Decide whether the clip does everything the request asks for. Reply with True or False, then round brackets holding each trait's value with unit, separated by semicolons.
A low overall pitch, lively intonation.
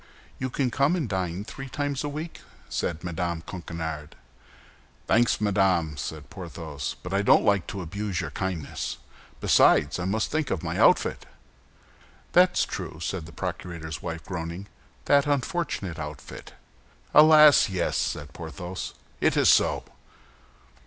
True (95 Hz; 8.0 semitones)